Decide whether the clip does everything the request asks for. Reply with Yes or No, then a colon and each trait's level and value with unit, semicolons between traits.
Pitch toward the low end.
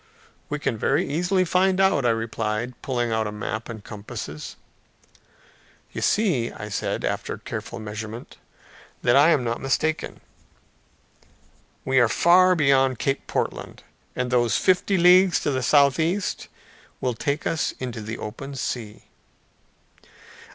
Yes: low, 130 Hz